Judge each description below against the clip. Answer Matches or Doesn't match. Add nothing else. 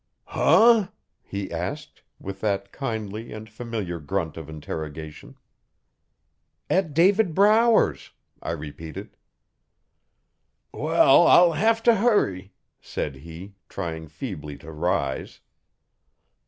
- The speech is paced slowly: Matches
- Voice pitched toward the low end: Matches